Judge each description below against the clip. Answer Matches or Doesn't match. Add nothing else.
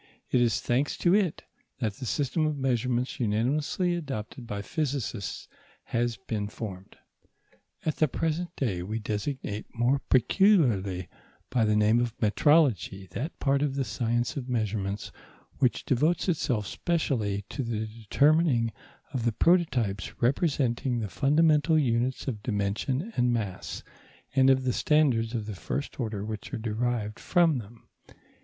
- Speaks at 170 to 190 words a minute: Doesn't match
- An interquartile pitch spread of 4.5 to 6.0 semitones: Matches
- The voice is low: Matches